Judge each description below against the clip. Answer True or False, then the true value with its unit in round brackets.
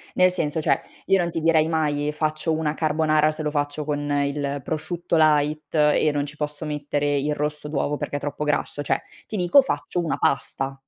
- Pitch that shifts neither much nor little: False (1.4 semitones)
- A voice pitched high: False (150 Hz)